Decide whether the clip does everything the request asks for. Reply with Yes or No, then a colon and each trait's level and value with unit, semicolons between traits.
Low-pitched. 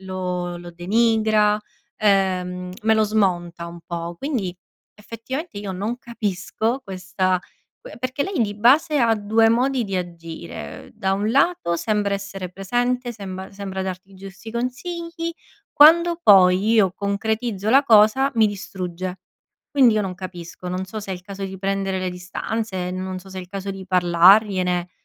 No: high, 195 Hz